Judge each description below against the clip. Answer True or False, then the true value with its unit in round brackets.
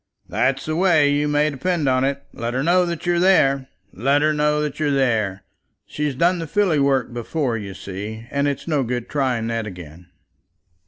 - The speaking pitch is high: False (140 Hz)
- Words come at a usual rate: True (195 wpm)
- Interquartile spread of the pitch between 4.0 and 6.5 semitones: True (4.3 semitones)